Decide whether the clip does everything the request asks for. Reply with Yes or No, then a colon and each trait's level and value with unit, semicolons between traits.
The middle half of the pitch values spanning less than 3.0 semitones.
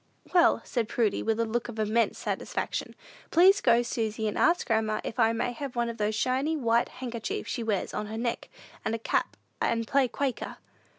Yes: narrow, 2.4 semitones